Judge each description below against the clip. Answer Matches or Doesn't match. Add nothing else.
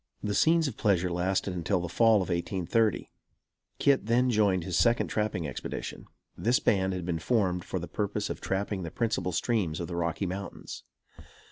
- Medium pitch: Doesn't match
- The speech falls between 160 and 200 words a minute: Matches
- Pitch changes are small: Doesn't match